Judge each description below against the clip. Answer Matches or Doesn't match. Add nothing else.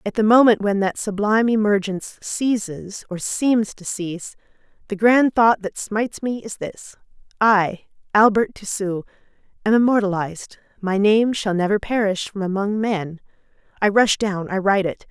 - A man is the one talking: Doesn't match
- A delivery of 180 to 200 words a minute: Doesn't match